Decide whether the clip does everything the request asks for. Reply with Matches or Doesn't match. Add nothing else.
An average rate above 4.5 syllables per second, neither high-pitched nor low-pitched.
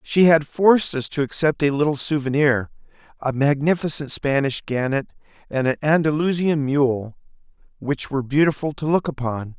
Matches